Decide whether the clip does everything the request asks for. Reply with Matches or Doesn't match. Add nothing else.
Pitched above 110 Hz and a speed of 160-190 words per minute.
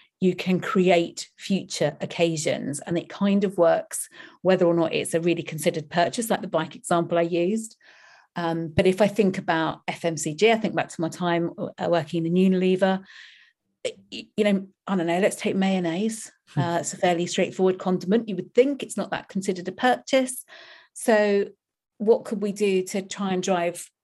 Matches